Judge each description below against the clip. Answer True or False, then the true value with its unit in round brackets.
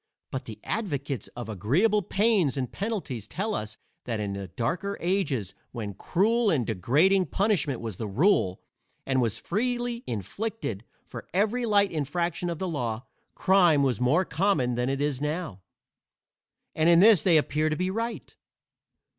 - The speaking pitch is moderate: True (155 Hz)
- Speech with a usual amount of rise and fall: False (8.3 semitones)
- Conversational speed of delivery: True (155 wpm)